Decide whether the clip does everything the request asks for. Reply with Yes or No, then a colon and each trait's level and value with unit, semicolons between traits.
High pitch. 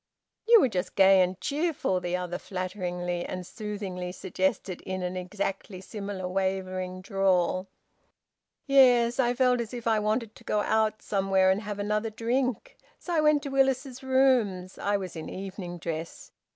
Yes: high, 200 Hz